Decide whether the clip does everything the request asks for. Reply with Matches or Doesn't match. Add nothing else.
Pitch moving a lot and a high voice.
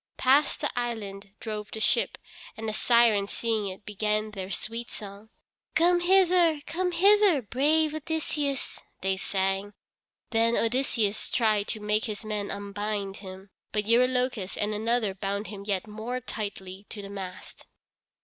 Doesn't match